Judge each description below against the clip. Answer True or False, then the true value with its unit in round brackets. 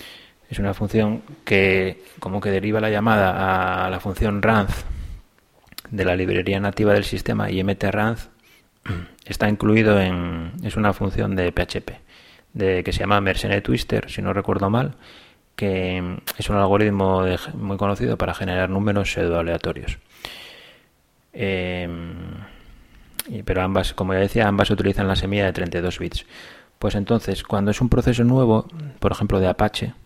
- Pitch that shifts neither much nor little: False (2.1 semitones)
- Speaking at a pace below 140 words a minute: False (150 wpm)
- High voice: False (100 Hz)